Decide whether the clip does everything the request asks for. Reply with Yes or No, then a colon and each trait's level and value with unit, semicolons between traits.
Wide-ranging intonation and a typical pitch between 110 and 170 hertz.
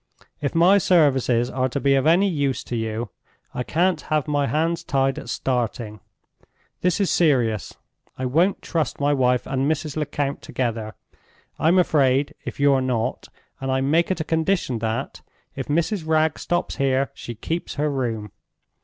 No: average, 4.0 semitones; medium, 140 Hz